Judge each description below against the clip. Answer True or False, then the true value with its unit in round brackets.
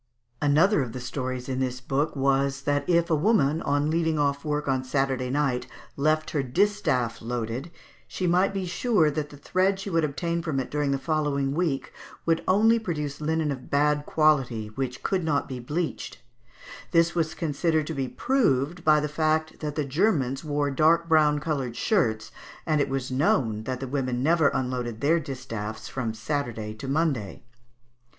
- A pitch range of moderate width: True (3.6 semitones)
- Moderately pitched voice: True (145 Hz)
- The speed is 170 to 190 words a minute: True (175 wpm)